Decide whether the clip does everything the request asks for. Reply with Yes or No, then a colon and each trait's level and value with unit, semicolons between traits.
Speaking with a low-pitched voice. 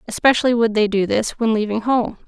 No: high, 225 Hz